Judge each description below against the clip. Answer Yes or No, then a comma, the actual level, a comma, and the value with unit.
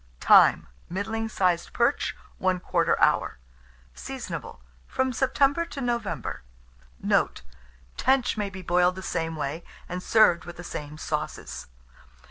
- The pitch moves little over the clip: No, wide, 5.6 semitones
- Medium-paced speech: No, slow, 120 wpm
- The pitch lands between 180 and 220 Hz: Yes, medium, 185 Hz